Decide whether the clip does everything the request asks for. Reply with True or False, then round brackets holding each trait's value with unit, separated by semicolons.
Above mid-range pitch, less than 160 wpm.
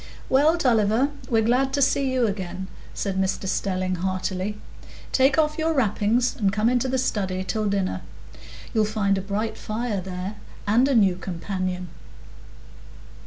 True (210 Hz; 150 wpm)